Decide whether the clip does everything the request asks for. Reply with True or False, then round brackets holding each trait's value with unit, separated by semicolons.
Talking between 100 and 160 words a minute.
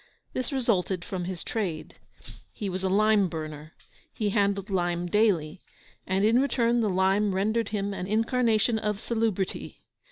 True (150 wpm)